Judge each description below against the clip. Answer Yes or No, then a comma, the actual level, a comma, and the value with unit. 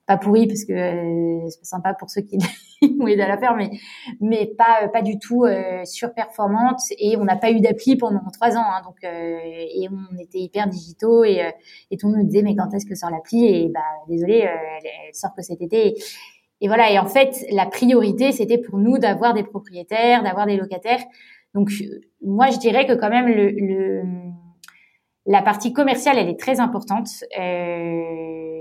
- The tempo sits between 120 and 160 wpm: No, average, 205 wpm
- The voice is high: Yes, high, 205 Hz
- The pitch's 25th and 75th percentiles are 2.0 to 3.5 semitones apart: No, average, 4.2 semitones